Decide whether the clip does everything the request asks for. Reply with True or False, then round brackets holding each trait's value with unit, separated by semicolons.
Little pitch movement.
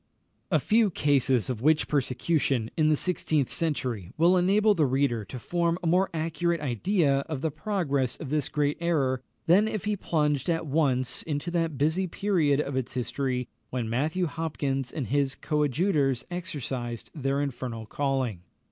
False (4.3 semitones)